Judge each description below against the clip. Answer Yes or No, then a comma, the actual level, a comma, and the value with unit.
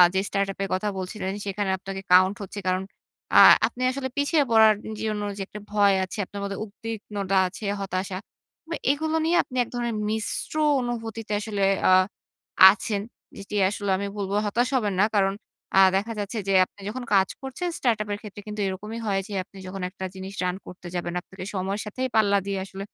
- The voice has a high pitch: Yes, high, 205 Hz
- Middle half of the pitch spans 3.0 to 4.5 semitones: No, narrow, 2.4 semitones